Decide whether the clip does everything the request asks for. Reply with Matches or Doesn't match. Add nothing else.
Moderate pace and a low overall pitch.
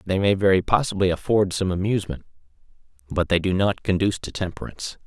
Matches